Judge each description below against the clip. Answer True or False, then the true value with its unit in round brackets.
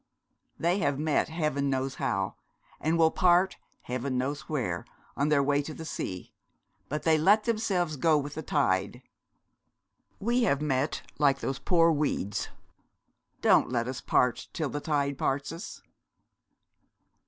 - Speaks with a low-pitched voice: False (145 Hz)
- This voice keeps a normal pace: True (145 wpm)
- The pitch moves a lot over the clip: False (3.4 semitones)